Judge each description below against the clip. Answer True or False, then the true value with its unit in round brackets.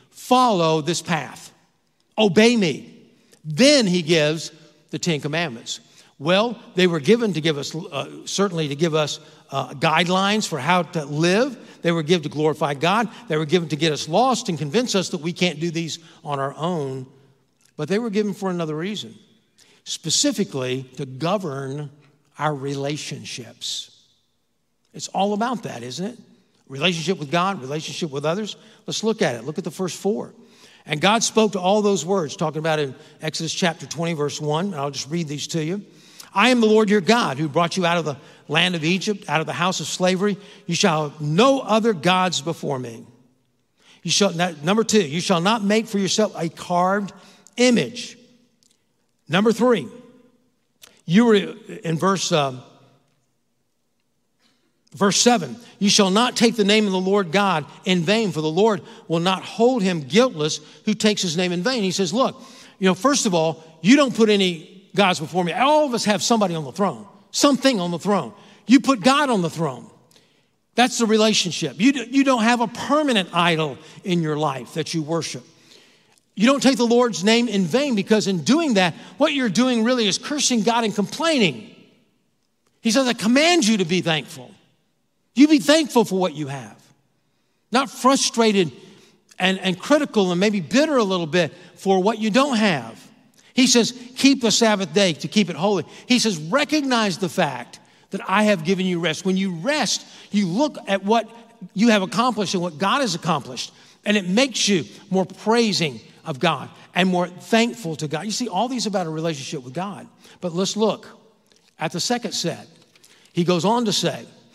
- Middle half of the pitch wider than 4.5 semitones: True (5.6 semitones)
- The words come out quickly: False (190 wpm)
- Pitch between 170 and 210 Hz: True (190 Hz)